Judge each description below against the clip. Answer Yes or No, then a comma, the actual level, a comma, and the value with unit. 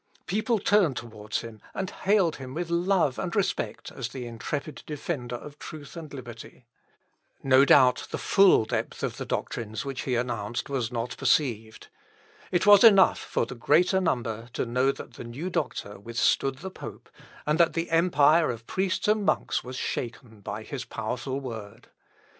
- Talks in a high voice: No, low, 135 Hz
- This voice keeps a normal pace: Yes, average, 170 wpm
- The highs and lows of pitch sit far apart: Yes, wide, 6.5 semitones